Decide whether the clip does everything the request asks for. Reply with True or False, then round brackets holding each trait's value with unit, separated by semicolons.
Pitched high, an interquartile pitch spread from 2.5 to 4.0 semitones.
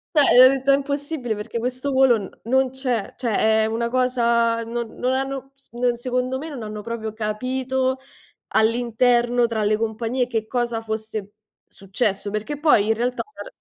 True (240 Hz; 2.8 semitones)